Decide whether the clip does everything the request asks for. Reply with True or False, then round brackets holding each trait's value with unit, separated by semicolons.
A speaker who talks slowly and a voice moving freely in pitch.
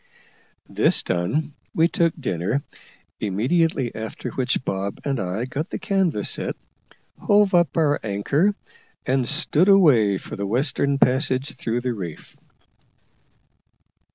True (125 wpm; 7.1 semitones)